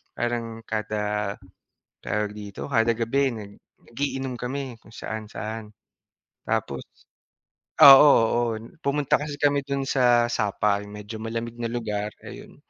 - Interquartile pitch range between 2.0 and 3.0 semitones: No, average, 3.4 semitones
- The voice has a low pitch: Yes, low, 115 Hz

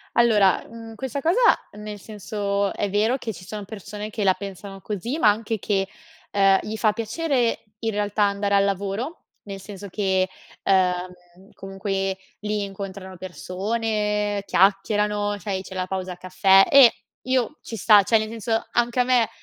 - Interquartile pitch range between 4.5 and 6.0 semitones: No, narrow, 2.4 semitones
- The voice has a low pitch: No, high, 205 Hz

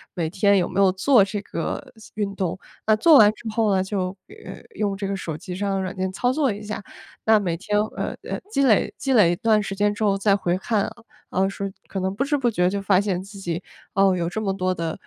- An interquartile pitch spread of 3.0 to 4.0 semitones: No, narrow, 2.4 semitones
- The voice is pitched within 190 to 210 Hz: Yes, high, 200 Hz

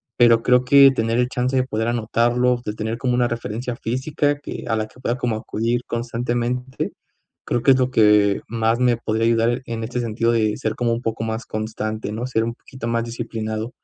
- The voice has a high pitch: No, low, 115 Hz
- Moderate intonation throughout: No, narrow, 1.8 semitones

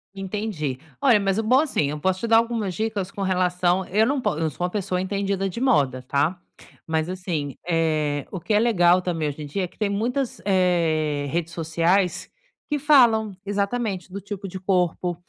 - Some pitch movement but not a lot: Yes, average, 4.1 semitones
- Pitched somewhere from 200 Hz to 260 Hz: No, medium, 185 Hz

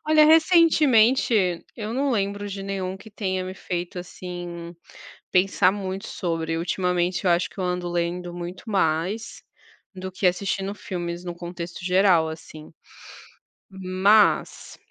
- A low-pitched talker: No, medium, 185 Hz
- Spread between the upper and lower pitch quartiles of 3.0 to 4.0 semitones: No, narrow, 2.5 semitones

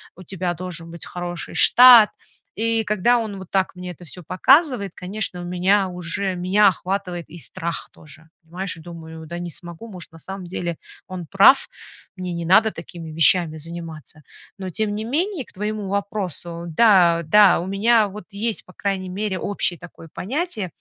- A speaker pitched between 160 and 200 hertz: Yes, medium, 185 Hz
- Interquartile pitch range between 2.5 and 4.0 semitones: Yes, average, 3.3 semitones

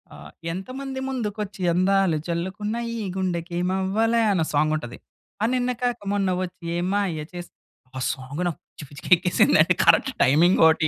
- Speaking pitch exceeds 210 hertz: No, medium, 185 Hz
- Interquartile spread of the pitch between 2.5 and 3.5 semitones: No, average, 4.2 semitones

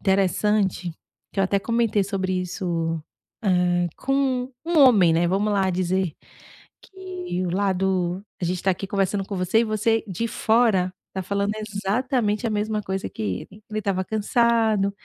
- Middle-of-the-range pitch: No, high, 200 Hz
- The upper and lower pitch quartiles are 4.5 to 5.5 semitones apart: No, average, 2.9 semitones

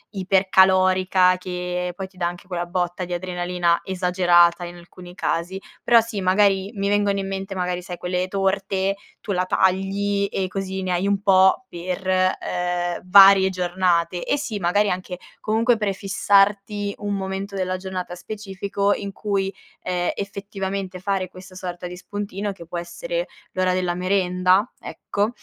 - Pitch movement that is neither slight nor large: No, narrow, 1.7 semitones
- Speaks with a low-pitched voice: No, high, 190 Hz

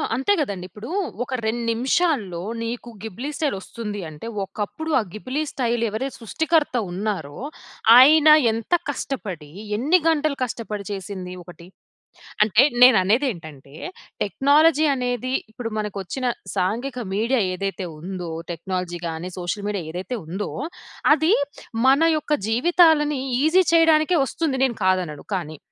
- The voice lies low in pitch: No, high, 225 Hz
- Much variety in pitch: Yes, wide, 6.8 semitones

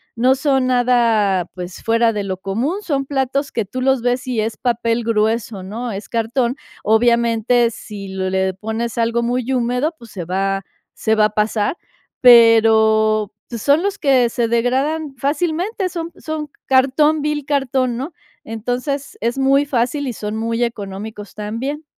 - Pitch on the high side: Yes, high, 235 Hz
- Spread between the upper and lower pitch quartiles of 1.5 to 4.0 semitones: Yes, average, 3.7 semitones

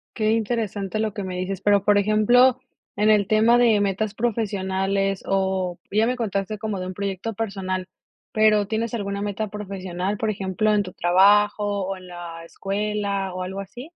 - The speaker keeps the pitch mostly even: Yes, narrow, 2.1 semitones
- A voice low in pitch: No, high, 200 Hz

